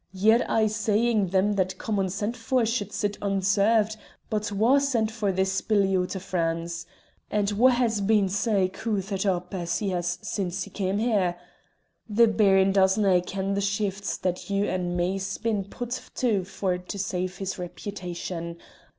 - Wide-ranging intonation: No, narrow, 2.5 semitones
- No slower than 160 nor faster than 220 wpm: Yes, average, 165 wpm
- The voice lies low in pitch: No, high, 195 Hz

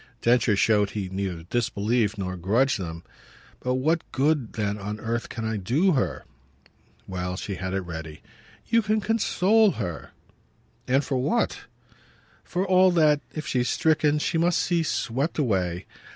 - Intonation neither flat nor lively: No, wide, 8.3 semitones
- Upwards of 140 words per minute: Yes, average, 150 wpm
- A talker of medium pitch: No, low, 120 Hz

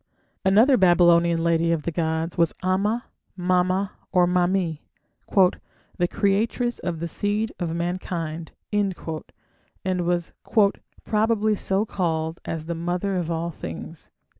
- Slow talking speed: Yes, slow, 120 wpm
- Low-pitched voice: No, medium, 175 Hz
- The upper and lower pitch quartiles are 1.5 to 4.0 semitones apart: Yes, average, 2.7 semitones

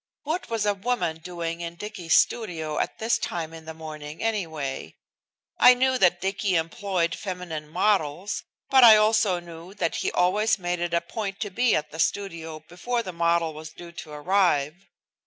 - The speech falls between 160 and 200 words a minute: Yes, average, 175 wpm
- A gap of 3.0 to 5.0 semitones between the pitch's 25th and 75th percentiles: Yes, average, 4.2 semitones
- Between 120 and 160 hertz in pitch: No, medium, 175 Hz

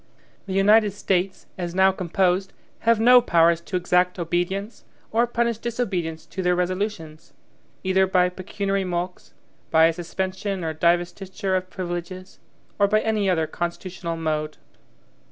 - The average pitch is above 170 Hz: Yes, medium, 185 Hz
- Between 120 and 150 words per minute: Yes, slow, 135 wpm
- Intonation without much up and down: Yes, narrow, 2.3 semitones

